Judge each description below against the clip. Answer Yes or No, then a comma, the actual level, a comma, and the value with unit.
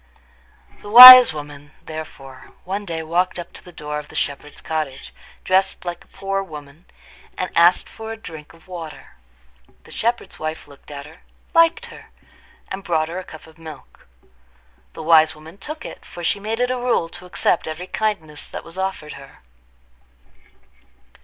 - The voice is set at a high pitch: No, medium, 170 Hz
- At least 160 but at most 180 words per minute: Yes, average, 170 wpm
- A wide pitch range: No, average, 4.0 semitones